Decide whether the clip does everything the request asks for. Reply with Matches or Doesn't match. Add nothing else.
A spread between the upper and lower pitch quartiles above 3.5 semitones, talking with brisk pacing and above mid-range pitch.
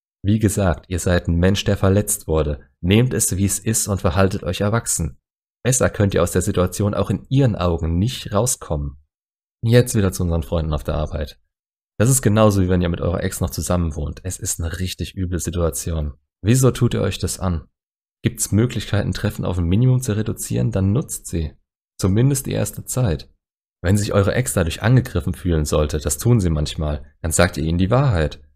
Doesn't match